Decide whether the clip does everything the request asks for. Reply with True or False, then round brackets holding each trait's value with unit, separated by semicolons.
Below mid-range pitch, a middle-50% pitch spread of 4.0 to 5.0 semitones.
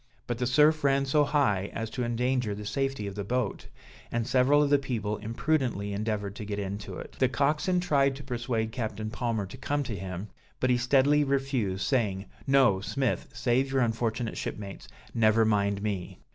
True (120 Hz; 4.6 semitones)